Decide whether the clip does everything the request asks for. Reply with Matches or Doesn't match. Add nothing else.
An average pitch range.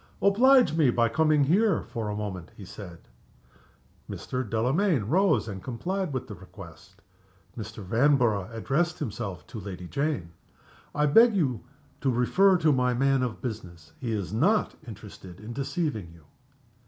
Doesn't match